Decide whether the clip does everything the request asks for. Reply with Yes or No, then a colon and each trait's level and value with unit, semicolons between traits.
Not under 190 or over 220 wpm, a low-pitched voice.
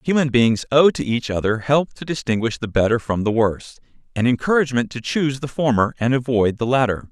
Yes: fast, 205 wpm; low, 125 Hz